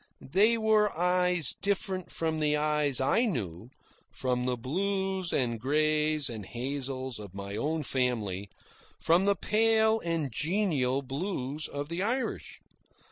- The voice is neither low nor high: Yes, medium, 150 Hz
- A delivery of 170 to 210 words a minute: No, slow, 135 wpm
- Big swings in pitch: Yes, wide, 6.9 semitones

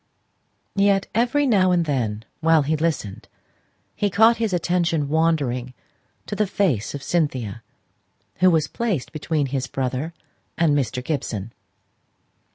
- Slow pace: Yes, slow, 130 wpm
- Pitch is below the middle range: No, medium, 160 Hz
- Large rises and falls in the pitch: Yes, wide, 6.0 semitones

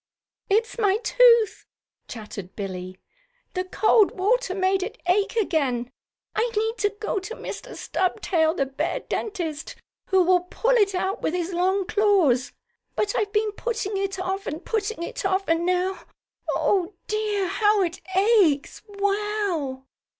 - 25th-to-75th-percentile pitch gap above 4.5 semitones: No, average, 3.5 semitones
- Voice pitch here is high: Yes, very high, 385 Hz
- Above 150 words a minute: No, average, 145 wpm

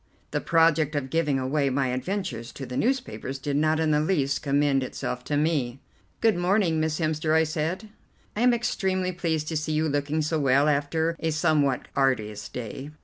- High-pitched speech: No, medium, 155 Hz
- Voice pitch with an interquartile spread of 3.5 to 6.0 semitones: No, average, 2.9 semitones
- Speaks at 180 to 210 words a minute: Yes, average, 185 wpm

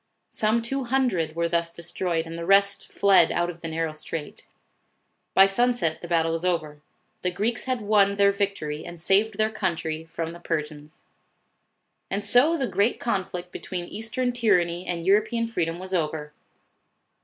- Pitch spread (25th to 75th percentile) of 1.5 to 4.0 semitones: No, average, 4.4 semitones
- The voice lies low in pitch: No, medium, 180 Hz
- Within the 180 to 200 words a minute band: No, average, 165 wpm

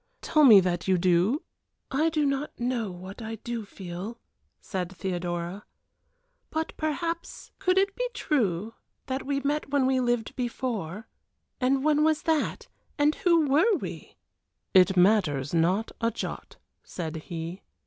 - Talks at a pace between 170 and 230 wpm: No, average, 150 wpm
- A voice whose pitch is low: No, high, 235 Hz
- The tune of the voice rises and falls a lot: Yes, wide, 8.0 semitones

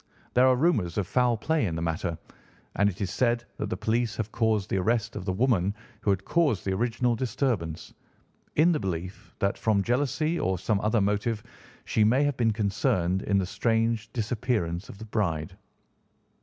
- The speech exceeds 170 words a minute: Yes, average, 185 wpm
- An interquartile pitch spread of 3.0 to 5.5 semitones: Yes, average, 4.1 semitones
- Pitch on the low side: Yes, low, 110 Hz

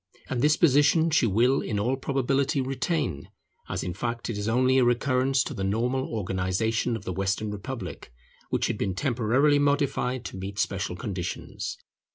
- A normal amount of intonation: Yes, average, 5.0 semitones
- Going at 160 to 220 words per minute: Yes, average, 170 wpm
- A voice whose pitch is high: No, low, 120 Hz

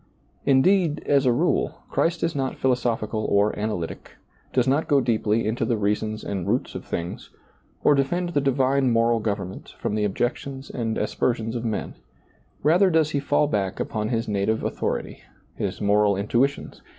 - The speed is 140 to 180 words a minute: Yes, average, 165 wpm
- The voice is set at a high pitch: No, low, 120 Hz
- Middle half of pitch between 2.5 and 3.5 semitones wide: No, average, 4.6 semitones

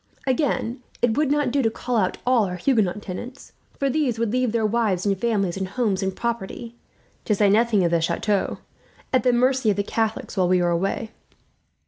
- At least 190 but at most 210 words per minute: Yes, average, 200 wpm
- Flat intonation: No, average, 4.1 semitones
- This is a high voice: Yes, high, 225 Hz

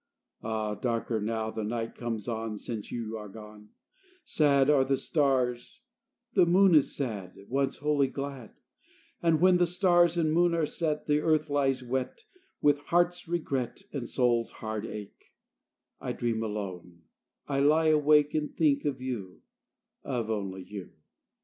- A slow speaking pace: No, average, 150 wpm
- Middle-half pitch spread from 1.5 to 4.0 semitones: No, wide, 5.4 semitones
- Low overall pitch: Yes, low, 130 Hz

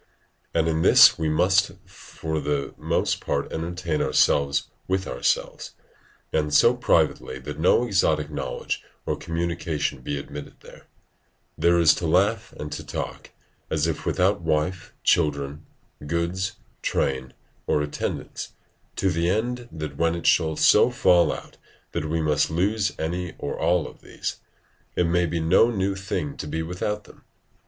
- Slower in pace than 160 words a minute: Yes, average, 150 wpm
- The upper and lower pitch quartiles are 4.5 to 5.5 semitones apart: No, average, 3.4 semitones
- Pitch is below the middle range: Yes, very low, 80 Hz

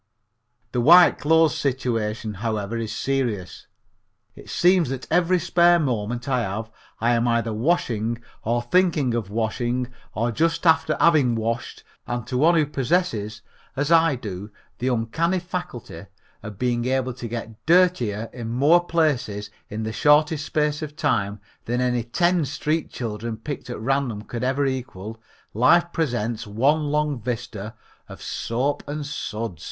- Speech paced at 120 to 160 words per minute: Yes, average, 150 wpm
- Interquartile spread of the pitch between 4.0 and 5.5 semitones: Yes, average, 5.2 semitones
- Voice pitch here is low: Yes, low, 125 Hz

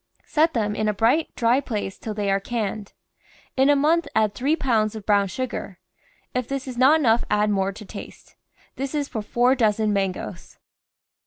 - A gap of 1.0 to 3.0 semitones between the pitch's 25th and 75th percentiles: No, average, 4.2 semitones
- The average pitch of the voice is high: Yes, high, 225 Hz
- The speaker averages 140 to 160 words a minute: No, average, 185 wpm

